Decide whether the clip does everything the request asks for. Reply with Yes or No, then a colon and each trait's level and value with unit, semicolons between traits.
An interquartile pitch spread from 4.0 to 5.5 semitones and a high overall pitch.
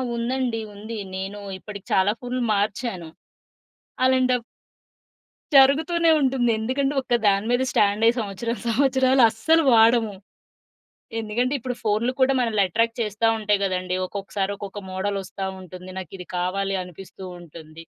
Yes: average, 4.3 semitones; high, 220 Hz